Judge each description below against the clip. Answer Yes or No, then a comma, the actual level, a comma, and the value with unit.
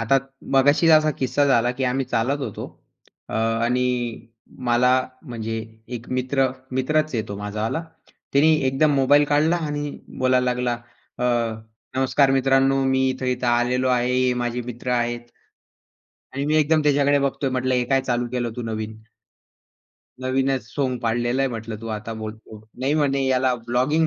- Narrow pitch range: Yes, narrow, 2.3 semitones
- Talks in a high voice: No, low, 130 Hz